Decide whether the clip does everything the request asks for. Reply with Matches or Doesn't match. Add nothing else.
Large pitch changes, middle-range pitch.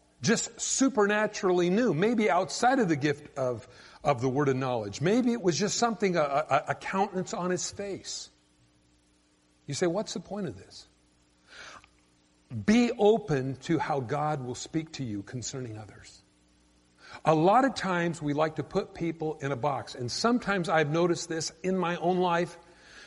Matches